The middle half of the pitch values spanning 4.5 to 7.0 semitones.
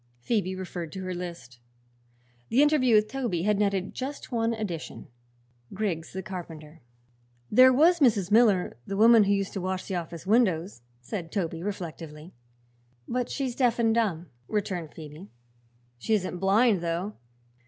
Yes: average, 4.9 semitones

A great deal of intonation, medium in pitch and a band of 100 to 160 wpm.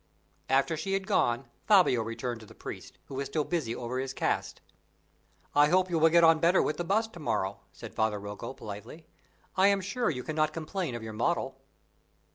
No: wide, 6.5 semitones; medium, 155 Hz; average, 200 wpm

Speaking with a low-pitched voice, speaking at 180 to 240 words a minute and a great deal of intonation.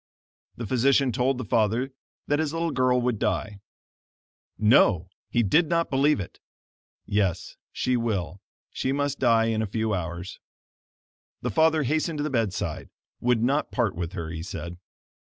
No: low, 120 Hz; average, 155 wpm; wide, 5.8 semitones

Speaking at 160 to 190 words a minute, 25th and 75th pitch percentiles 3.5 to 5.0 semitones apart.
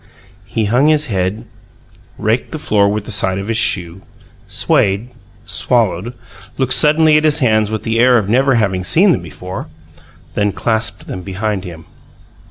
Yes: average, 165 wpm; average, 4.4 semitones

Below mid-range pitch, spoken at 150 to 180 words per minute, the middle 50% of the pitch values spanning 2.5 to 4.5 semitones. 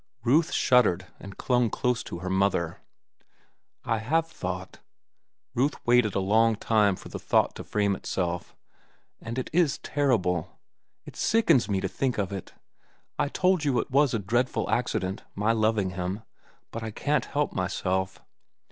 No: low, 110 Hz; average, 155 wpm; average, 5.1 semitones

